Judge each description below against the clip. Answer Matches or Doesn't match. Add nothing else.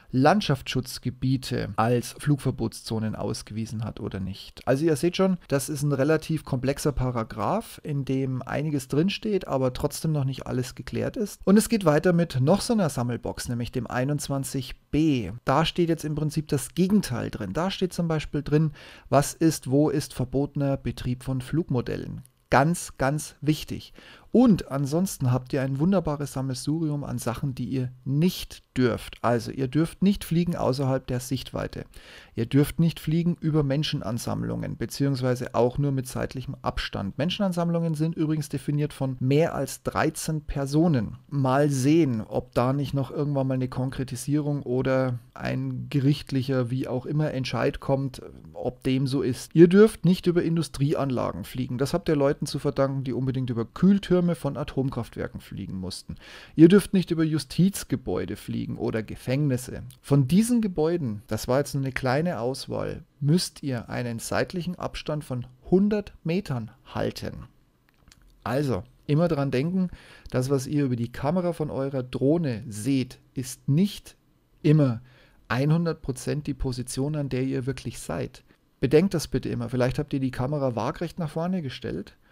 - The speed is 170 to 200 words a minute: Doesn't match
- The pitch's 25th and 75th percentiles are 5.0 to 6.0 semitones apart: Doesn't match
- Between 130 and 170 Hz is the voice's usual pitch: Matches